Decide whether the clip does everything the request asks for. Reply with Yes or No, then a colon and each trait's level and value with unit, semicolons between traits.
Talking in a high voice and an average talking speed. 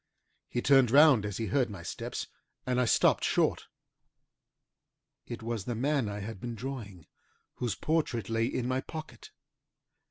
No: low, 120 Hz; average, 155 wpm